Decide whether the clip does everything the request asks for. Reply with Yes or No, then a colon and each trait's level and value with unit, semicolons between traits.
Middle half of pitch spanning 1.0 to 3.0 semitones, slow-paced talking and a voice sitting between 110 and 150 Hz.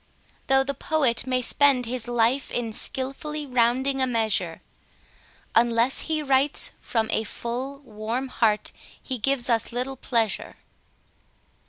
No: average, 2.7 semitones; slow, 130 wpm; very high, 250 Hz